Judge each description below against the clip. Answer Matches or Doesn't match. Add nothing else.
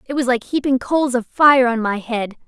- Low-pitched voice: Doesn't match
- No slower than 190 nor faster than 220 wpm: Doesn't match